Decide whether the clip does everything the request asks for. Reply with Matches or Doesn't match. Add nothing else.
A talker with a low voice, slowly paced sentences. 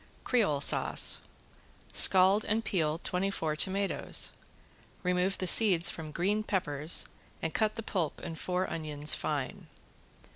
Doesn't match